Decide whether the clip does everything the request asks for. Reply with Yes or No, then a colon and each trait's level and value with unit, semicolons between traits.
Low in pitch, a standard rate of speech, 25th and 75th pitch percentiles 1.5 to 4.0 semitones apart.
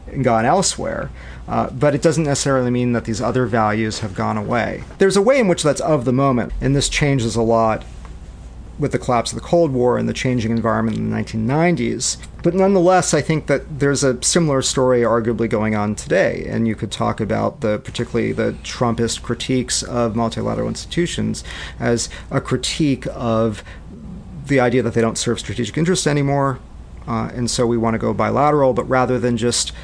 Yes: low, 120 Hz; average, 190 wpm; average, 3.7 semitones